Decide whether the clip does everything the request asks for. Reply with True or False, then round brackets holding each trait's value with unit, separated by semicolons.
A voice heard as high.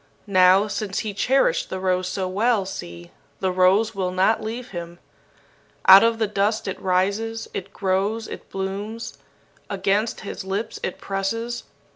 True (195 Hz)